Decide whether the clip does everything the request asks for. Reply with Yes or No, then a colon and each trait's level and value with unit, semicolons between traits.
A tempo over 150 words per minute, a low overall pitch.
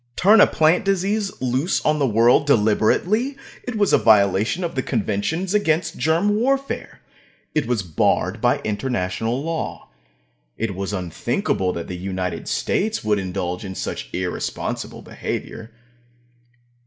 No: slow, 135 wpm; low, 125 Hz